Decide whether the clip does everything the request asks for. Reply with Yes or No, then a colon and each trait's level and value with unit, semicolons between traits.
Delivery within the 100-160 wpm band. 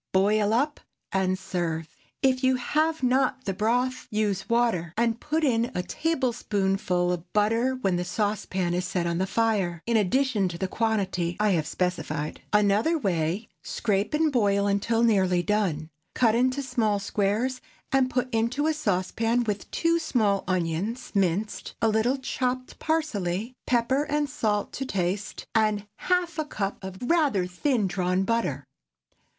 Yes: average, 155 wpm